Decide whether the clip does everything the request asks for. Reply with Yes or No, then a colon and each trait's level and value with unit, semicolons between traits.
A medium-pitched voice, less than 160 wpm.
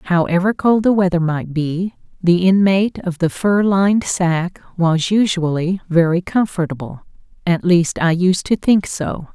Yes: medium, 180 Hz; average, 150 wpm